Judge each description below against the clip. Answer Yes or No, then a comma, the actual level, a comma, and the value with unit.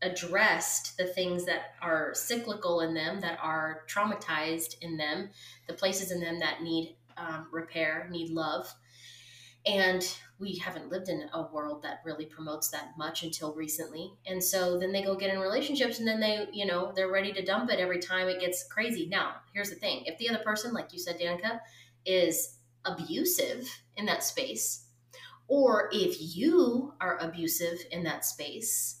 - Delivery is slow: No, average, 175 wpm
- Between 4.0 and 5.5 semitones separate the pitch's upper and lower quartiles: No, average, 3.5 semitones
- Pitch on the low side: No, medium, 175 Hz